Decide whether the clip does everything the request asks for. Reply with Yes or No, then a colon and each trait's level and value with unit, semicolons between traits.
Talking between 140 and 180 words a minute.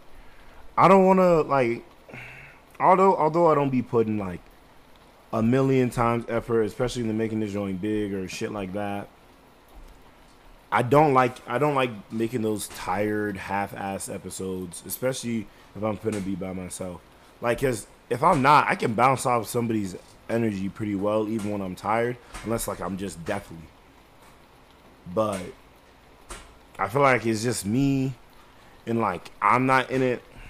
Yes: average, 155 wpm